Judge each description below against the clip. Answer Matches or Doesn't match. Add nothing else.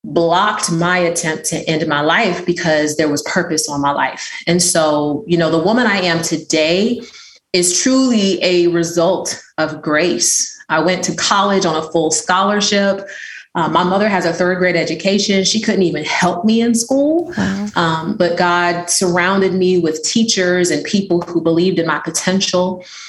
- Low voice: Doesn't match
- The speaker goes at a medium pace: Matches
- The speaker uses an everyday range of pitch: Matches